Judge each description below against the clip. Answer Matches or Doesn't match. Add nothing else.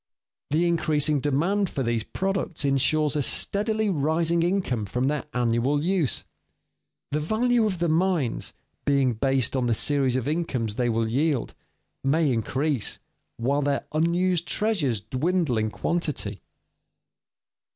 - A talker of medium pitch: Matches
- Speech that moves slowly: Matches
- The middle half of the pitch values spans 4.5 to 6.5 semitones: Matches